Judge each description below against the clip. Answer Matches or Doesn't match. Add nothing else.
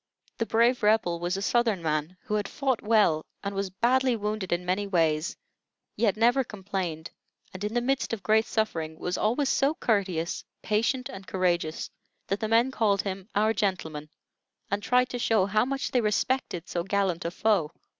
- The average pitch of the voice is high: Matches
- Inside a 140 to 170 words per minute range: Doesn't match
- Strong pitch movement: Doesn't match